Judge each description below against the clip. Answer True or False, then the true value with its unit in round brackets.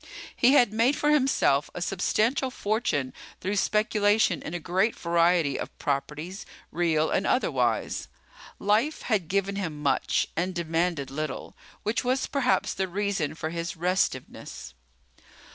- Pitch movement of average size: True (5.0 semitones)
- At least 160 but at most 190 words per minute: False (135 wpm)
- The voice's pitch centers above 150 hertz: True (185 Hz)